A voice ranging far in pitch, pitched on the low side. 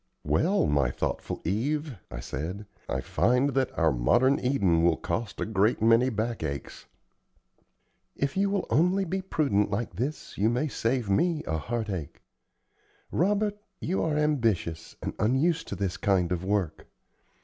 Yes: wide, 8.4 semitones; low, 115 Hz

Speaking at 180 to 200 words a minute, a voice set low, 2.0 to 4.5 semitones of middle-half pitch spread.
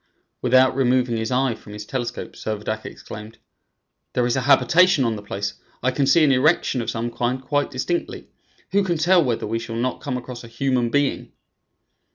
Yes: average, 190 wpm; low, 125 Hz; average, 2.9 semitones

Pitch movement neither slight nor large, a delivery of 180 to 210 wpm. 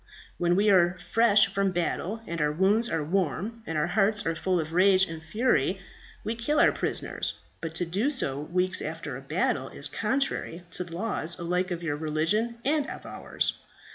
Yes: average, 4.5 semitones; average, 190 wpm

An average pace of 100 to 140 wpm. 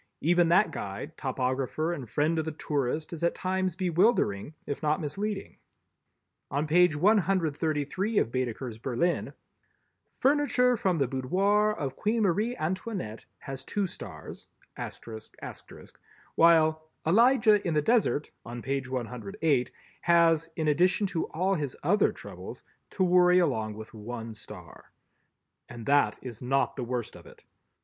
Yes: slow, 135 wpm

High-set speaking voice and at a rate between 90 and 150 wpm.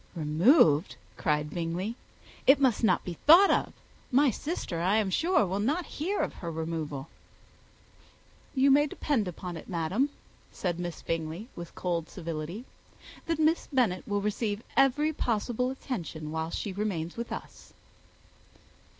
Yes: high, 200 Hz; average, 140 wpm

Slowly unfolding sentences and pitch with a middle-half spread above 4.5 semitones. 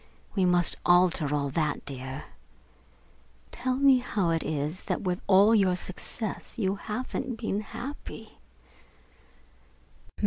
Yes: slow, 115 wpm; wide, 5.5 semitones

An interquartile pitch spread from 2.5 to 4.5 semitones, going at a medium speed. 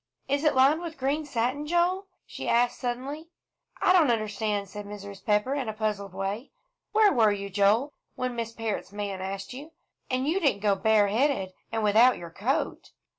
No: wide, 5.5 semitones; average, 175 wpm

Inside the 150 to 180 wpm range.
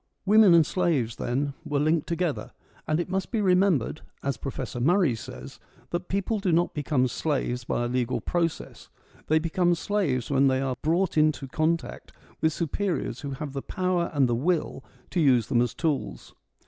Yes: average, 175 wpm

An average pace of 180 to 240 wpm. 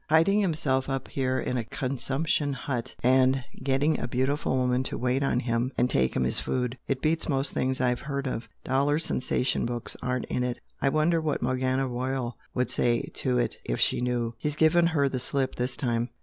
Yes: average, 200 wpm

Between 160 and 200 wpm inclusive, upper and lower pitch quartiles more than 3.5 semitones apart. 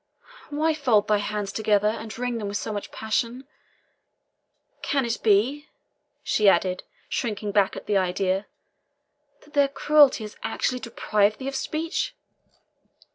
No: average, 140 wpm; average, 4.7 semitones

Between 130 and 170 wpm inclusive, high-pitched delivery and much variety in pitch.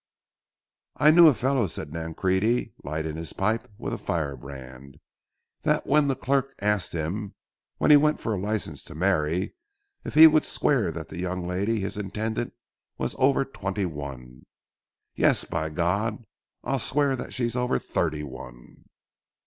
No: average, 150 wpm; very low, 95 Hz; wide, 7.7 semitones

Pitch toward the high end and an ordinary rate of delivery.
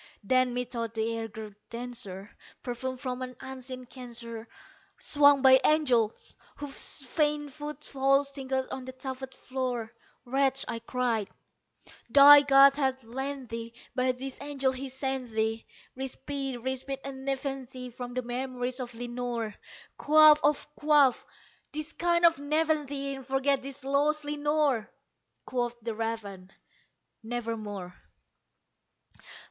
No: very high, 260 Hz; slow, 125 wpm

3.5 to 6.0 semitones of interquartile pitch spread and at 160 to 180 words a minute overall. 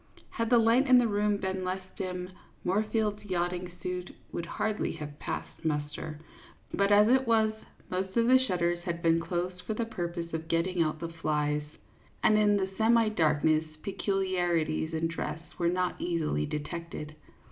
Yes: average, 4.0 semitones; average, 170 wpm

